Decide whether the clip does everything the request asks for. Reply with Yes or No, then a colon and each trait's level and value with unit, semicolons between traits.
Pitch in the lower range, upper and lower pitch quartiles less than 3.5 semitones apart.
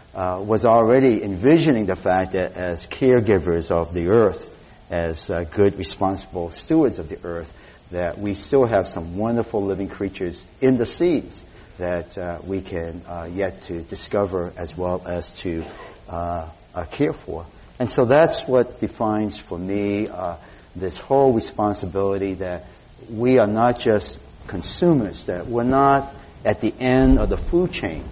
No: very low, 95 Hz; average, 4.5 semitones